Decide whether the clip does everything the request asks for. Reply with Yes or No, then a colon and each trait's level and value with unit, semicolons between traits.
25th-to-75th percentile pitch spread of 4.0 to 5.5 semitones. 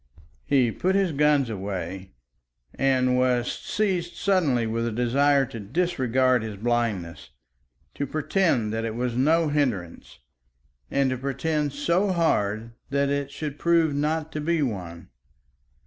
Yes: average, 4.9 semitones